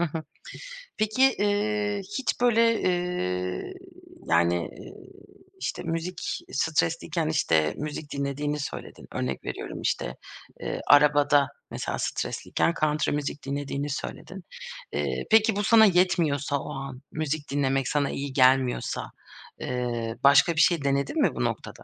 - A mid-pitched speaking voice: Yes, medium, 145 Hz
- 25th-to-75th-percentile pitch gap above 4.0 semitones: Yes, average, 4.5 semitones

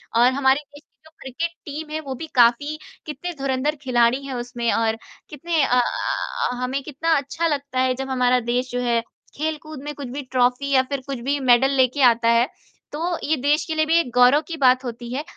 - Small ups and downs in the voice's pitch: No, average, 3.2 semitones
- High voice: Yes, very high, 265 Hz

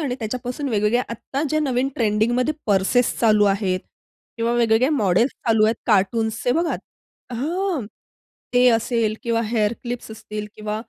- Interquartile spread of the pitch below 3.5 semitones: Yes, average, 2.8 semitones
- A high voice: Yes, high, 230 Hz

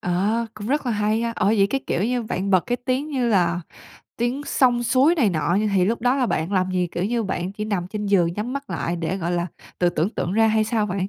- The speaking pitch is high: Yes, high, 210 Hz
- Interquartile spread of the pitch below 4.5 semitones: No, average, 4.9 semitones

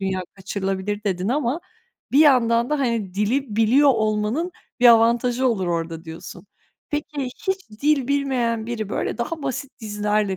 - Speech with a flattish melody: No, average, 4.6 semitones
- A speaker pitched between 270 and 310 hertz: No, high, 230 Hz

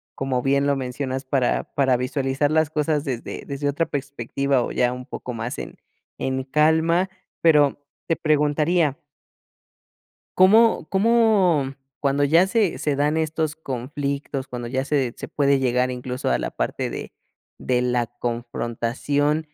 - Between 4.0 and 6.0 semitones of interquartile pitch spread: No, average, 3.3 semitones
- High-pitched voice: No, medium, 140 Hz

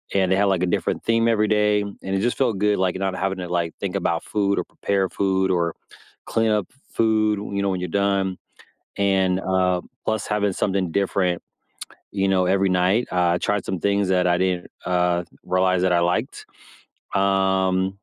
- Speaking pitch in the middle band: No, very low, 95 Hz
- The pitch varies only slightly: Yes, narrow, 1.7 semitones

